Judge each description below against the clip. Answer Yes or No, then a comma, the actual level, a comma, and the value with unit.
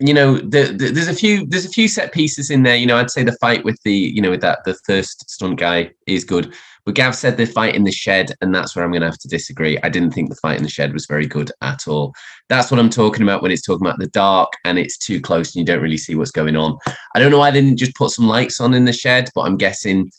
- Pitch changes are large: Yes, wide, 6.4 semitones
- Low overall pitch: Yes, low, 110 Hz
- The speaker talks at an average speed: No, fast, 305 wpm